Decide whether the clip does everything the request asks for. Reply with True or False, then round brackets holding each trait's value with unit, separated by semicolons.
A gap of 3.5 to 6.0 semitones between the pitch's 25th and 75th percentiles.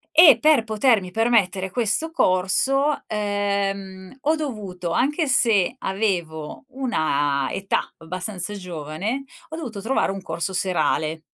True (5.5 semitones)